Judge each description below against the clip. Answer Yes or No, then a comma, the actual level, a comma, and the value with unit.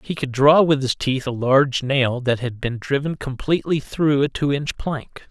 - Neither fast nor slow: No, fast, 215 wpm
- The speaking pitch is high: No, low, 135 Hz